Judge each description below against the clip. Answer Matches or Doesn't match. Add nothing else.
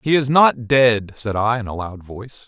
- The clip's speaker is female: Doesn't match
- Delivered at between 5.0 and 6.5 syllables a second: Doesn't match